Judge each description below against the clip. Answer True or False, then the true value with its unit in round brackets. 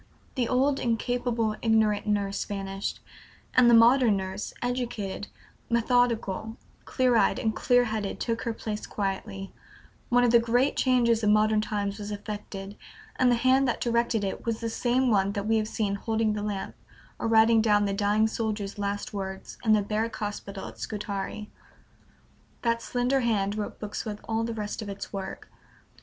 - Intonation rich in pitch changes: False (2.4 semitones)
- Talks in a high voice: True (220 Hz)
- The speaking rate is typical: True (170 wpm)